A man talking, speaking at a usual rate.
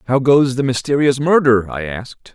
Yes: male; average, 180 wpm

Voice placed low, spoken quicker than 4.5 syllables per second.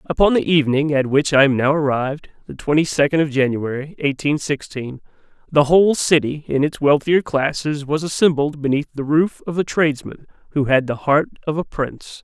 No: medium, 145 Hz; 5.4 syllables/s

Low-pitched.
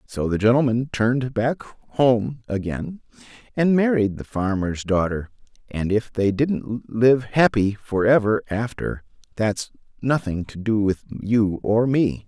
Yes: low, 115 Hz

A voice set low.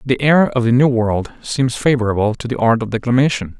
Yes: low, 120 Hz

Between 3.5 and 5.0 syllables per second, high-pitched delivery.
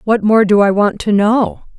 Yes: 4.6 syllables/s; high, 210 Hz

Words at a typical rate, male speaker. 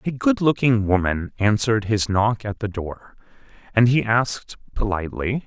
Yes: average, 155 wpm; male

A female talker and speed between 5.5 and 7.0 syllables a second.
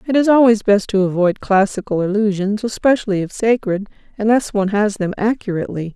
Yes: female; 5.8 syllables/s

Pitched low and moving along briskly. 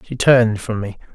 Yes: low, 110 Hz; fast, 210 wpm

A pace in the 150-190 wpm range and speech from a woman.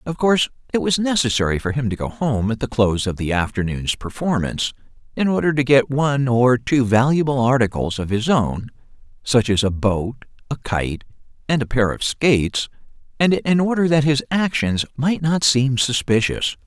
No: average, 175 wpm; male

